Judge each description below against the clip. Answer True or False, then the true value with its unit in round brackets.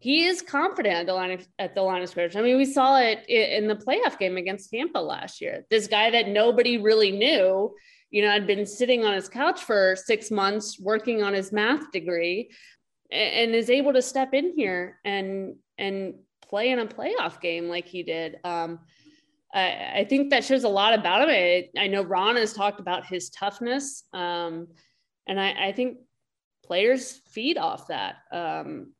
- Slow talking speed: False (190 wpm)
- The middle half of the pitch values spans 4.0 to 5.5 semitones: True (5.2 semitones)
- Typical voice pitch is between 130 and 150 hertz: False (210 Hz)